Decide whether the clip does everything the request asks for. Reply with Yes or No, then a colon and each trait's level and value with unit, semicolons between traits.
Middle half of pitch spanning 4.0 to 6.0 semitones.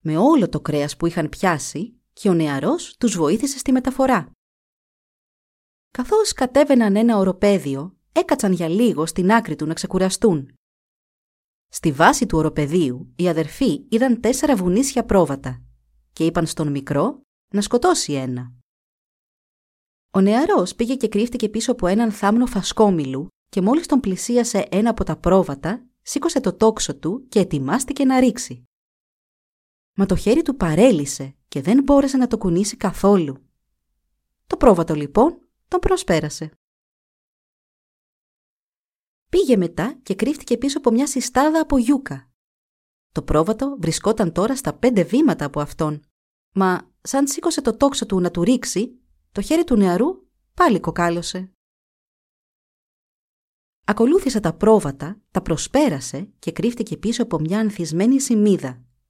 No: wide, 7.9 semitones